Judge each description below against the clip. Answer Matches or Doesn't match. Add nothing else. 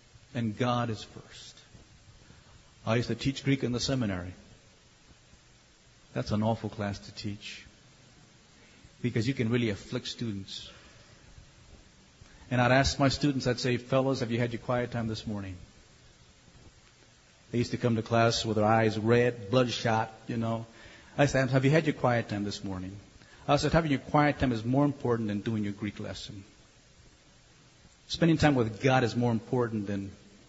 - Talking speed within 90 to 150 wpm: Doesn't match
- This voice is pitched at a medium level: Doesn't match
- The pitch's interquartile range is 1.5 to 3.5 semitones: Matches